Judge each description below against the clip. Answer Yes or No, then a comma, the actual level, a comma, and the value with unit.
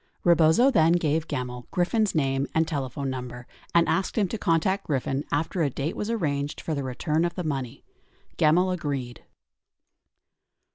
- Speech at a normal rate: Yes, average, 155 wpm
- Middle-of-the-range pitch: Yes, medium, 155 Hz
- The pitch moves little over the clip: No, average, 4.1 semitones